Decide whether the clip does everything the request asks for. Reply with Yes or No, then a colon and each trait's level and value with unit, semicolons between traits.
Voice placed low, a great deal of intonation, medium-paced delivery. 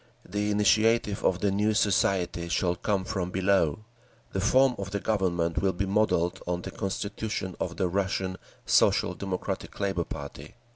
No: very low, 95 Hz; narrow, 2.5 semitones; average, 155 wpm